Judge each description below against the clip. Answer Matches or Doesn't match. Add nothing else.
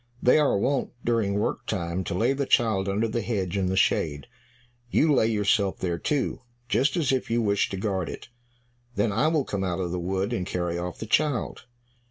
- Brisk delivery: Matches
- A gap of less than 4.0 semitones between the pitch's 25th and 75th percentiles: Doesn't match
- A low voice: Matches